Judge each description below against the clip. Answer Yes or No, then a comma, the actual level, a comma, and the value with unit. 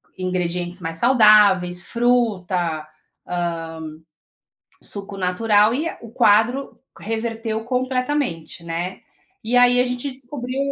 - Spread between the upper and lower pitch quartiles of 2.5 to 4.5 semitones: No, wide, 5.6 semitones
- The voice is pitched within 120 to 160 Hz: No, high, 215 Hz